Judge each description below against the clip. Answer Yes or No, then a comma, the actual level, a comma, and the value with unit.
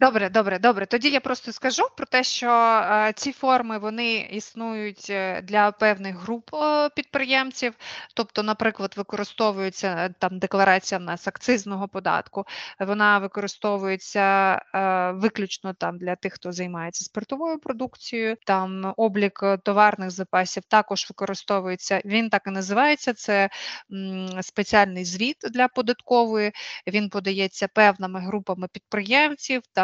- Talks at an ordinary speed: Yes, average, 115 wpm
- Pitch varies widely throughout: No, average, 3.3 semitones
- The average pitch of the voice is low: No, high, 210 Hz